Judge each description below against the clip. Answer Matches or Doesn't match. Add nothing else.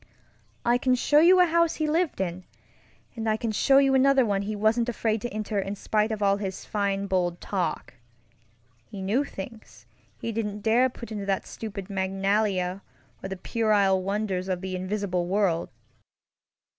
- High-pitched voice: Matches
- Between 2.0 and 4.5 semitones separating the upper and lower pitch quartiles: Matches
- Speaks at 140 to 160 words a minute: Doesn't match